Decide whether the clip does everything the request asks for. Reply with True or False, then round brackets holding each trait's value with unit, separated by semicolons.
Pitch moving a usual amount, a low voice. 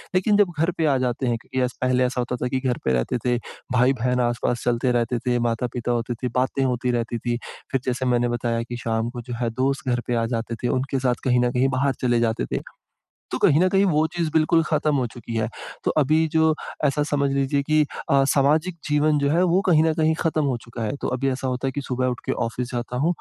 True (3.4 semitones; 130 Hz)